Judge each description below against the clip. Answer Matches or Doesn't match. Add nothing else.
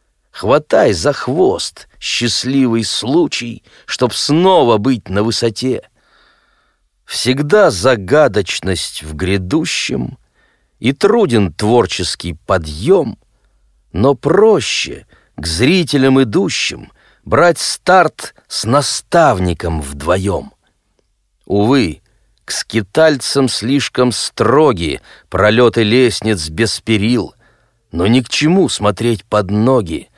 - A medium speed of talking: Doesn't match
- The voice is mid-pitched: Doesn't match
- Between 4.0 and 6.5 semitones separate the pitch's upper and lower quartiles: Matches